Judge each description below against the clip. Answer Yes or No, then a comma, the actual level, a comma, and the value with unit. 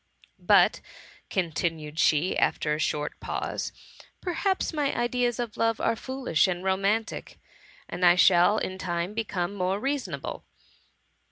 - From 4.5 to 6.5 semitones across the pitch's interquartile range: Yes, wide, 5.5 semitones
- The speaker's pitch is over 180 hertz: Yes, high, 190 Hz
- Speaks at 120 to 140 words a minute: Yes, slow, 135 wpm